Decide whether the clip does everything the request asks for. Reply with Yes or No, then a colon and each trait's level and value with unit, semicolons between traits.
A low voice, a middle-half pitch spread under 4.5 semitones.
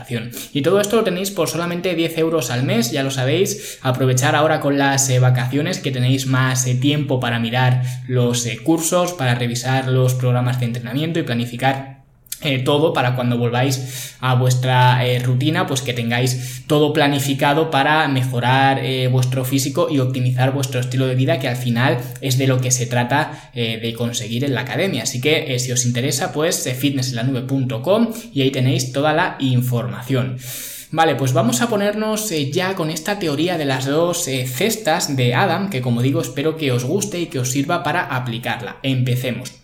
Yes: low, 130 Hz; average, 3.3 semitones